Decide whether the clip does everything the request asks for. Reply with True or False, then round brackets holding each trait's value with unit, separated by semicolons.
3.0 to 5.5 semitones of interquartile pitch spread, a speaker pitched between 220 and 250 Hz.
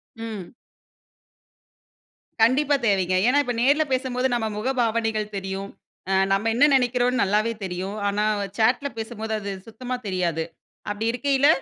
True (3.9 semitones; 225 Hz)